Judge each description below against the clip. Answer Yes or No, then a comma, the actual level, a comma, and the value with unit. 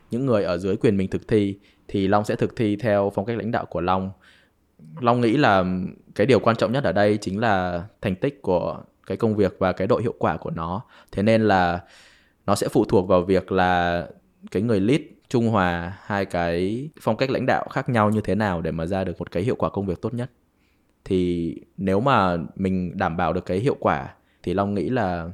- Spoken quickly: No, average, 230 wpm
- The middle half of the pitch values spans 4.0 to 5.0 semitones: No, average, 2.9 semitones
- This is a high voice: No, very low, 95 Hz